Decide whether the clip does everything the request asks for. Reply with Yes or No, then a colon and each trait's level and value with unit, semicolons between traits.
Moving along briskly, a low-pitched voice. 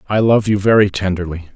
No: average, 190 wpm; low, 100 Hz